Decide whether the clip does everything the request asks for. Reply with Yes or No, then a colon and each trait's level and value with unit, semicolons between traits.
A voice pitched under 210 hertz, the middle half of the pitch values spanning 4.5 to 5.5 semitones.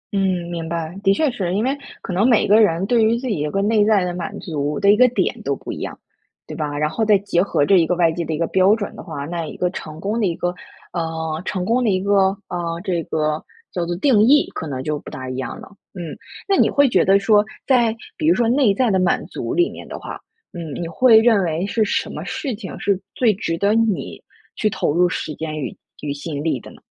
Yes: medium, 185 Hz; average, 4.8 semitones